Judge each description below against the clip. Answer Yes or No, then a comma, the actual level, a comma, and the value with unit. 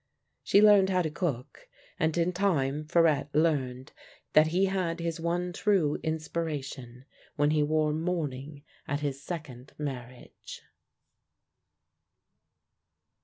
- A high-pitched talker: No, medium, 155 Hz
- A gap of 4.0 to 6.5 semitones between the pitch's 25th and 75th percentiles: No, average, 3.3 semitones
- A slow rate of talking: Yes, slow, 115 wpm